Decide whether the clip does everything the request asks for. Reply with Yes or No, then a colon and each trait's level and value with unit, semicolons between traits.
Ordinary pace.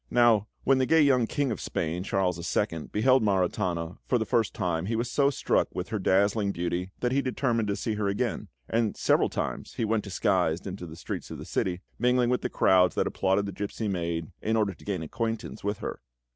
No: fast, 215 wpm